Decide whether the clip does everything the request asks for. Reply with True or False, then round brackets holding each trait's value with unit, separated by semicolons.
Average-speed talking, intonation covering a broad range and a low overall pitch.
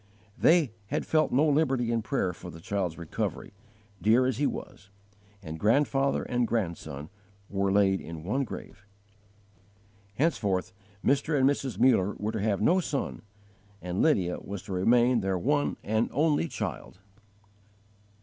True (145 wpm; 6.3 semitones; 110 Hz)